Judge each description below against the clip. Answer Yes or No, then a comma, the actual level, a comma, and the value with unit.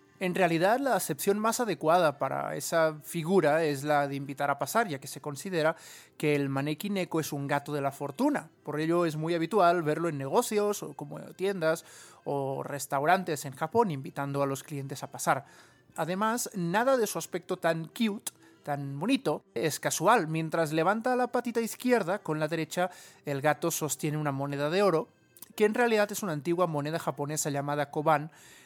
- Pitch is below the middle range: No, medium, 160 Hz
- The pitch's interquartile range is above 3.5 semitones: Yes, average, 4.7 semitones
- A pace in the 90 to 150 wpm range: No, average, 180 wpm